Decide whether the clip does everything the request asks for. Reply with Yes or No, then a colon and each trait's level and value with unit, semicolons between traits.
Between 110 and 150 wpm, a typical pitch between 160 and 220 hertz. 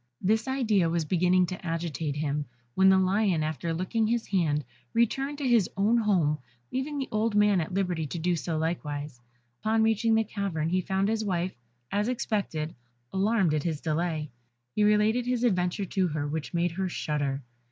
No: average, 185 wpm; medium, 185 Hz